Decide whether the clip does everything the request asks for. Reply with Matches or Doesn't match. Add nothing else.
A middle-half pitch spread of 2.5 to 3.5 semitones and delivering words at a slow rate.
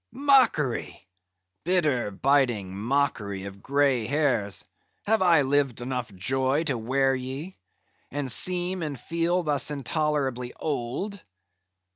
Doesn't match